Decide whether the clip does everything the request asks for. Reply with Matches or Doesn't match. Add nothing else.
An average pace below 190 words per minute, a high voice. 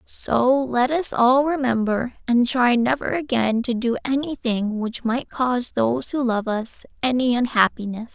Matches